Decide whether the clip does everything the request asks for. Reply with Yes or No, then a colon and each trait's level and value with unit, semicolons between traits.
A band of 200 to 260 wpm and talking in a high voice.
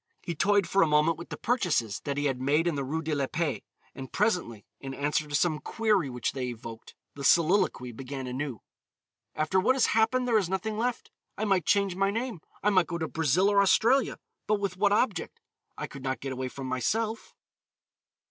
No: fast, 205 wpm; medium, 165 Hz